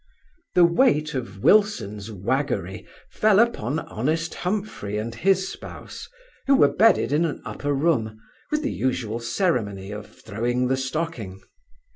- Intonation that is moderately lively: No, wide, 8.5 semitones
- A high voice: No, low, 135 Hz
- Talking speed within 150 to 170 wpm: No, slow, 135 wpm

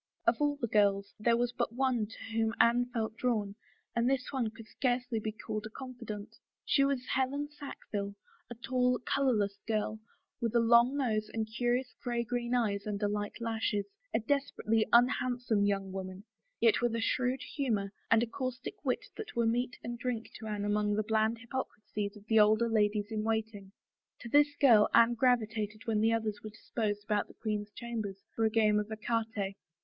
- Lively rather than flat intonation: No, narrow, 2.5 semitones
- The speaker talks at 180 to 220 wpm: Yes, average, 185 wpm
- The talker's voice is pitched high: Yes, high, 225 Hz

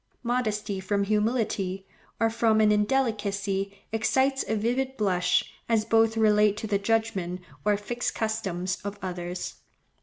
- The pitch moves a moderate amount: No, narrow, 2.3 semitones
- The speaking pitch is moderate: No, high, 210 Hz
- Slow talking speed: Yes, slow, 130 wpm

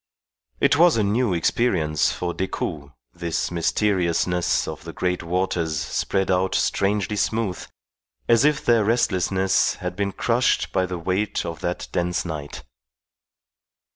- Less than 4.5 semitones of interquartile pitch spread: Yes, average, 3.5 semitones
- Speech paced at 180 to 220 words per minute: No, slow, 135 wpm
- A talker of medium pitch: No, very low, 95 Hz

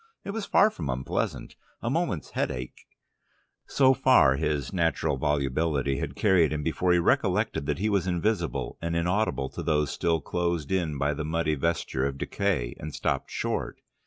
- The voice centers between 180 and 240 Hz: No, very low, 80 Hz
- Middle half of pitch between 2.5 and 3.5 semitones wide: No, average, 4.2 semitones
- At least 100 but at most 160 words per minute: No, average, 170 wpm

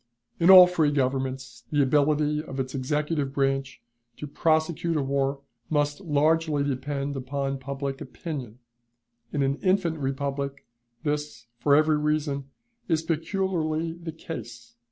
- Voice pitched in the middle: Yes, medium, 145 Hz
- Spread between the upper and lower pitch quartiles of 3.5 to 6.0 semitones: No, narrow, 2.5 semitones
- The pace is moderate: No, slow, 130 wpm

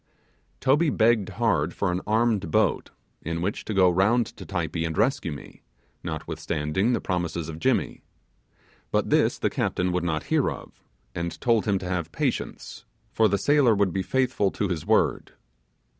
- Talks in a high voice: No, very low, 95 Hz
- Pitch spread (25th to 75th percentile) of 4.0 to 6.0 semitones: Yes, average, 4.8 semitones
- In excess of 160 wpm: Yes, average, 170 wpm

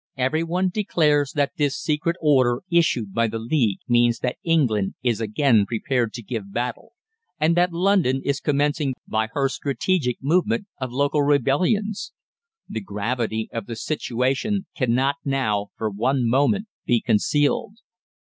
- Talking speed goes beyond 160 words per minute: No, average, 145 wpm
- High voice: No, low, 135 Hz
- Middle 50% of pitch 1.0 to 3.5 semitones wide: No, average, 5.2 semitones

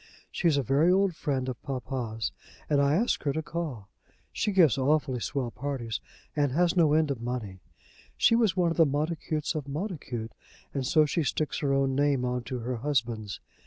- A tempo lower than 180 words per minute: No, average, 190 wpm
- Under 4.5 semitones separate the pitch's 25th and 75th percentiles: Yes, average, 4.0 semitones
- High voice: No, medium, 140 Hz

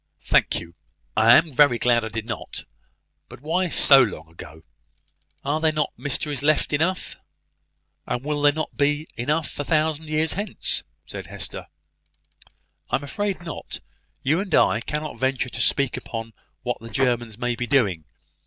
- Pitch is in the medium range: Yes, medium, 145 Hz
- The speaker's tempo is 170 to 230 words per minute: No, average, 160 wpm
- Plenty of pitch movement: No, average, 4.5 semitones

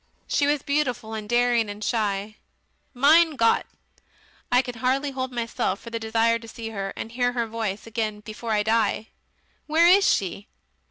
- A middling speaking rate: Yes, average, 170 wpm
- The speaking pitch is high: Yes, high, 230 Hz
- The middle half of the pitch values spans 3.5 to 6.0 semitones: No, average, 2.9 semitones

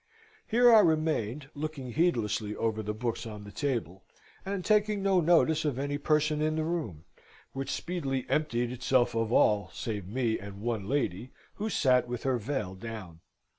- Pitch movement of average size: No, wide, 6.0 semitones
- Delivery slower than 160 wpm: No, average, 170 wpm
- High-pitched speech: No, low, 130 Hz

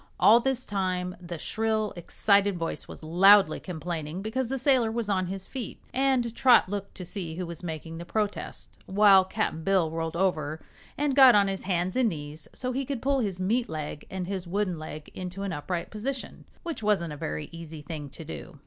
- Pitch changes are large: No, average, 5.0 semitones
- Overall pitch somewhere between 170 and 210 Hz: Yes, high, 190 Hz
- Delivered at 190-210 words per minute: Yes, average, 200 wpm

